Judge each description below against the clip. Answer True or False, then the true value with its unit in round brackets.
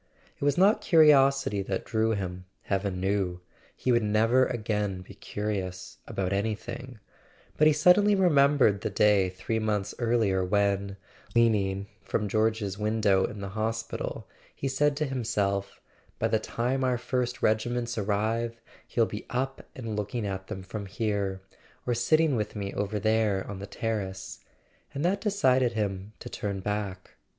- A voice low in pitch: True (110 Hz)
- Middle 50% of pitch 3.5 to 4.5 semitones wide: True (3.9 semitones)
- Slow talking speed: False (150 wpm)